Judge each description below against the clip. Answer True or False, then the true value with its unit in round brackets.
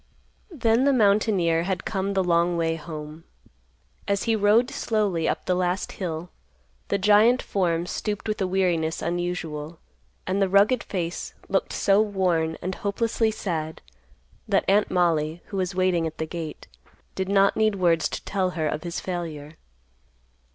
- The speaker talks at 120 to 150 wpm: False (160 wpm)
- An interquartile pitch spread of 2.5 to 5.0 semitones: True (3.4 semitones)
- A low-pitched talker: False (185 Hz)